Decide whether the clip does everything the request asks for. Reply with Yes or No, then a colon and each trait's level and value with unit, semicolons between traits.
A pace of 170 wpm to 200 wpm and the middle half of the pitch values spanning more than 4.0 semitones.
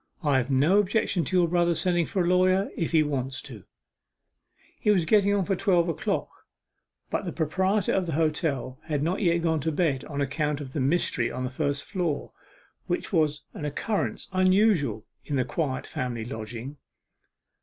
Yes: average, 180 wpm; average, 4.7 semitones